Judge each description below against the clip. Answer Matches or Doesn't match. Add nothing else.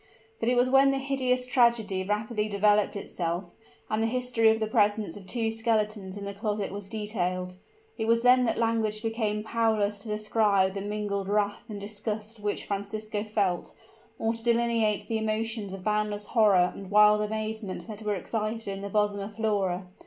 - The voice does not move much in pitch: Matches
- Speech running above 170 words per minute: Matches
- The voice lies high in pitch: Matches